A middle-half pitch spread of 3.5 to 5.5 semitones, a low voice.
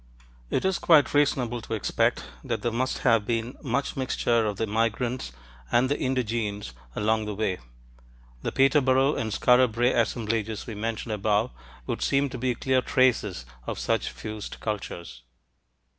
No: average, 3.1 semitones; low, 115 Hz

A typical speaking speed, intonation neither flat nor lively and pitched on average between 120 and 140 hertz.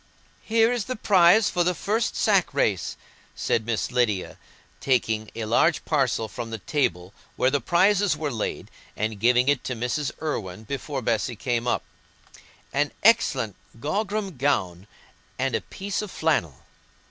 No: average, 150 wpm; wide, 8.0 semitones; low, 135 Hz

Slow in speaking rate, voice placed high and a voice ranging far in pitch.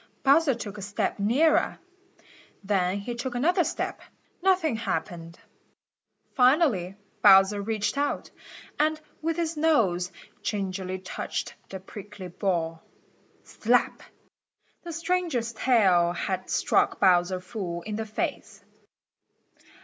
Yes: slow, 110 wpm; high, 210 Hz; wide, 7.3 semitones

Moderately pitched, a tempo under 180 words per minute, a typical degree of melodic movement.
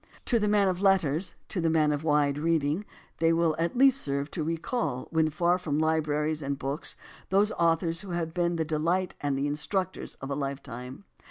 No: medium, 160 Hz; average, 195 wpm; average, 3.4 semitones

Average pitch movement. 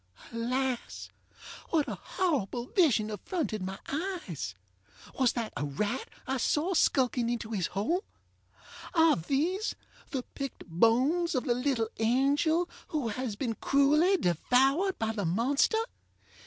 No: wide, 5.7 semitones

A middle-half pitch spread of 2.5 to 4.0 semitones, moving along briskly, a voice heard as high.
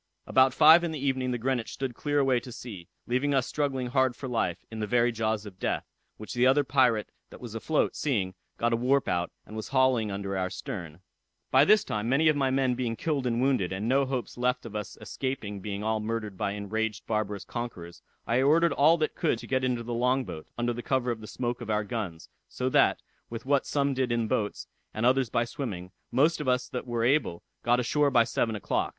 No: average, 3.5 semitones; fast, 230 wpm; low, 120 Hz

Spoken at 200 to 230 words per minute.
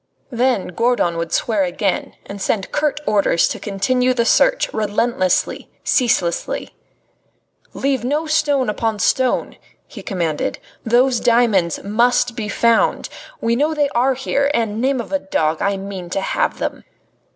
No: average, 145 wpm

